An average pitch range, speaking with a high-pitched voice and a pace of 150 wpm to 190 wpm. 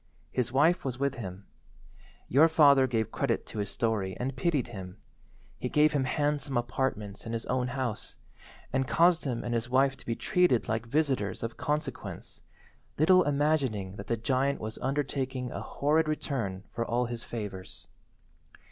No: average, 4.0 semitones; low, 130 Hz; average, 165 wpm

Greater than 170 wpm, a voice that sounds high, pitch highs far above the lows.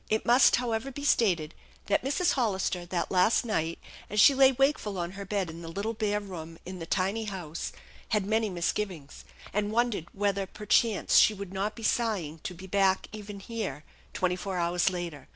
No: average, 190 wpm; high, 200 Hz; average, 3.6 semitones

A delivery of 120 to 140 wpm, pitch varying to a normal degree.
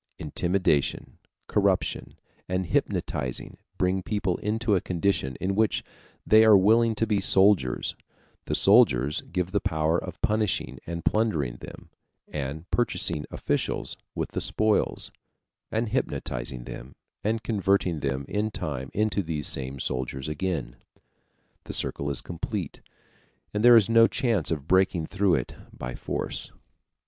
No: slow, 135 wpm; wide, 6.6 semitones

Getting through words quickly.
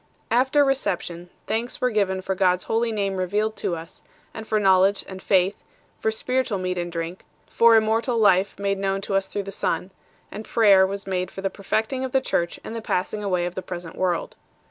Yes: fast, 215 wpm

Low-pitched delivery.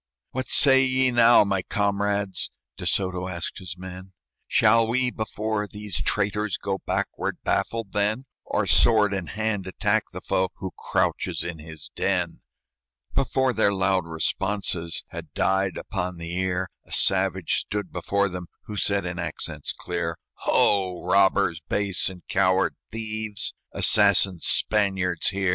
Yes: very low, 95 Hz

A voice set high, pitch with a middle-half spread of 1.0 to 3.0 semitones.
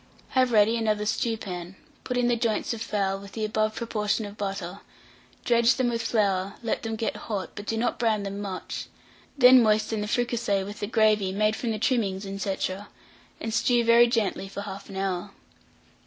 Yes: high, 215 Hz; narrow, 2.6 semitones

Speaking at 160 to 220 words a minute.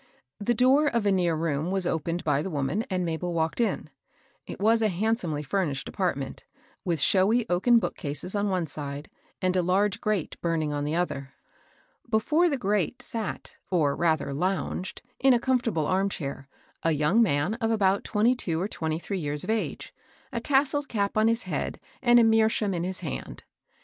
Yes: average, 185 wpm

